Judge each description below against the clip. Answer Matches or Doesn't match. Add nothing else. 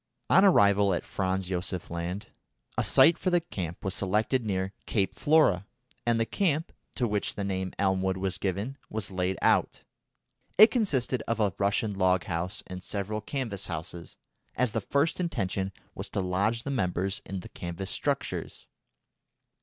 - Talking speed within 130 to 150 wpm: Doesn't match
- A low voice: Matches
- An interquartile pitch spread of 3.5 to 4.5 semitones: Matches